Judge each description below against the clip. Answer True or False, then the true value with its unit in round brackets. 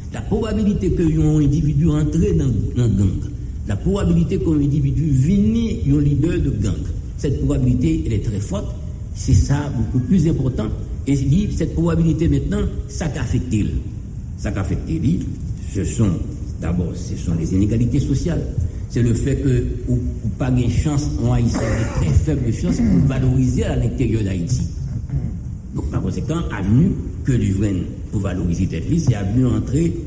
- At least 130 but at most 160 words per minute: True (155 wpm)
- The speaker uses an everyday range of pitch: False (6.4 semitones)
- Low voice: True (120 Hz)